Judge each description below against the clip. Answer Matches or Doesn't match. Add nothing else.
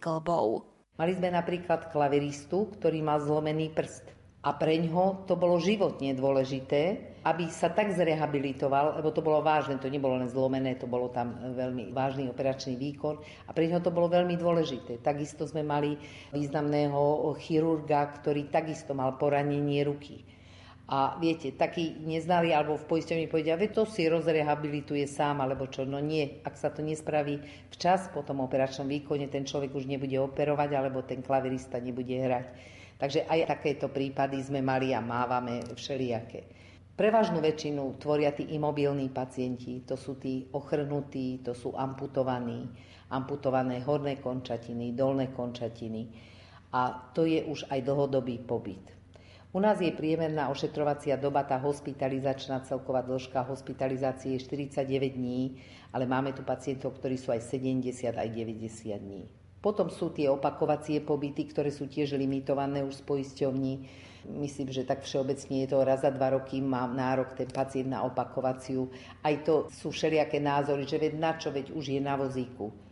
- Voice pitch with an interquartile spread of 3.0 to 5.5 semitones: Doesn't match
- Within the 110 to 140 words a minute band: Doesn't match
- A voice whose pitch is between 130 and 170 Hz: Matches